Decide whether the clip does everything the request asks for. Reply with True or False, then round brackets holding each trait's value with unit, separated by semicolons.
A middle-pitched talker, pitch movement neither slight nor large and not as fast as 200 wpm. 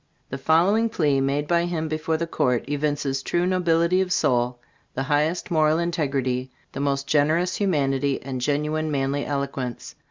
True (150 Hz; 3.4 semitones; 155 wpm)